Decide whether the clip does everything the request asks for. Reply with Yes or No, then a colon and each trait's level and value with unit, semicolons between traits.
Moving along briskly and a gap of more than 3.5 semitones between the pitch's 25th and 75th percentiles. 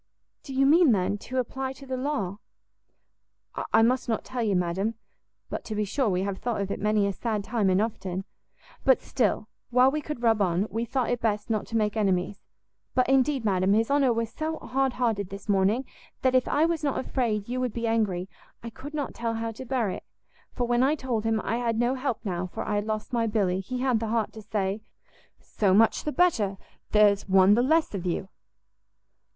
Yes: fast, 215 wpm; average, 4.1 semitones